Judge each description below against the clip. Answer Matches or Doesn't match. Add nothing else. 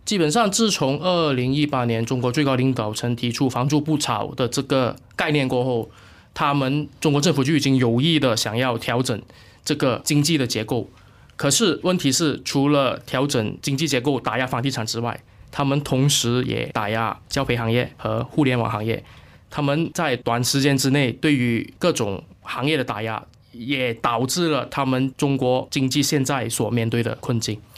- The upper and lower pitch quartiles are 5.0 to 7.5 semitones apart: Doesn't match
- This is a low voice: Matches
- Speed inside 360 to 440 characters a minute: Doesn't match